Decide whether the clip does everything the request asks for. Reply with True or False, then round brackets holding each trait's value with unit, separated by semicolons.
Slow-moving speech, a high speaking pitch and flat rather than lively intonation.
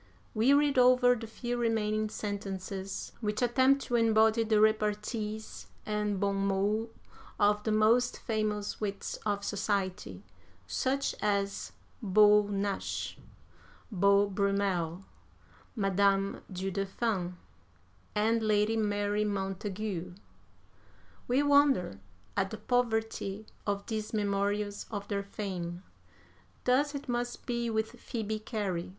True (110 wpm; 210 Hz; 2.1 semitones)